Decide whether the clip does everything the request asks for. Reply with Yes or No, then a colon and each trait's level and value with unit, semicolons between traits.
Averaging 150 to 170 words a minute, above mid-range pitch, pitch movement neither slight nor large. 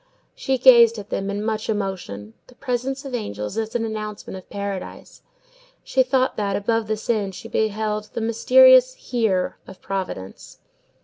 Yes: average, 160 wpm; high, 215 Hz; average, 3.4 semitones